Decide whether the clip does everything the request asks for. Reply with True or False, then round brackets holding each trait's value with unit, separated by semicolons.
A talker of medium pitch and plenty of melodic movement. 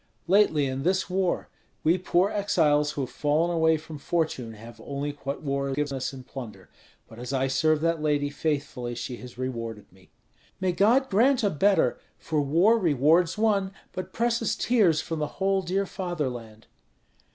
True (155 Hz; 5.7 semitones)